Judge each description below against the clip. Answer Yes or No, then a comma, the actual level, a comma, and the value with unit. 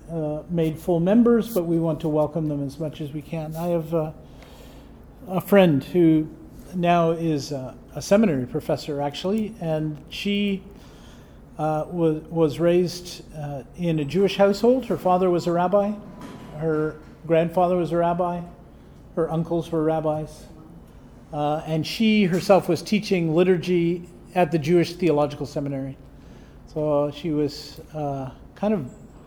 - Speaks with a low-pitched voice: No, medium, 165 Hz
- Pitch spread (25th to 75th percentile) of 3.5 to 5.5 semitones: No, average, 2.8 semitones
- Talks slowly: No, average, 145 wpm